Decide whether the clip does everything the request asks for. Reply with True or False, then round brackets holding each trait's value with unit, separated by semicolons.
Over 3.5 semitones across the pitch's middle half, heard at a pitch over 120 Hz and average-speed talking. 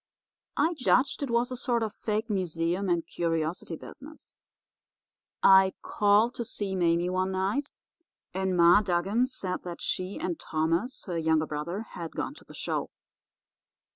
True (4.7 semitones; 190 Hz; 150 wpm)